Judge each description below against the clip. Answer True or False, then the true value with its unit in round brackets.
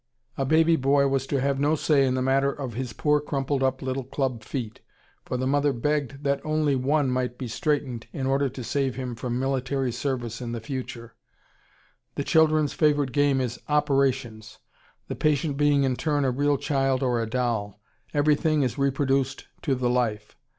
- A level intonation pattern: True (2.3 semitones)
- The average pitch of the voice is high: False (135 Hz)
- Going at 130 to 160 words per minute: False (185 wpm)